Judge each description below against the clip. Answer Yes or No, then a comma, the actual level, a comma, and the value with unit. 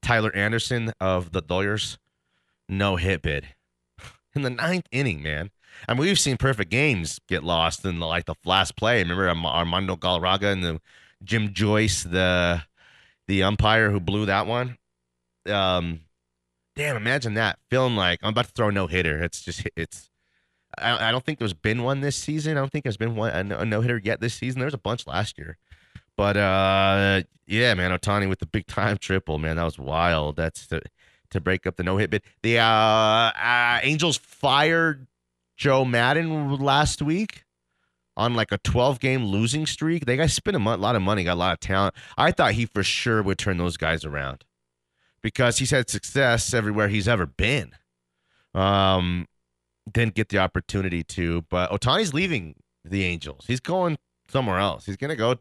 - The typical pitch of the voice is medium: No, low, 100 Hz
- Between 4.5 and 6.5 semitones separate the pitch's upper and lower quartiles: Yes, wide, 5.6 semitones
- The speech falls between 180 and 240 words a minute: Yes, average, 185 wpm